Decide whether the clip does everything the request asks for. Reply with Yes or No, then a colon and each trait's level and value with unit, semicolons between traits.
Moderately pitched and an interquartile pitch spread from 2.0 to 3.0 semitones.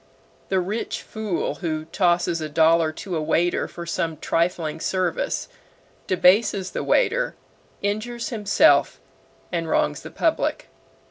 No: medium, 180 Hz; average, 3.7 semitones